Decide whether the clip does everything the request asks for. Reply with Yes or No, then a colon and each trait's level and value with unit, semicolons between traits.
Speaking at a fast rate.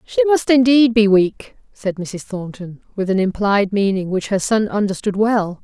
No: average, 180 wpm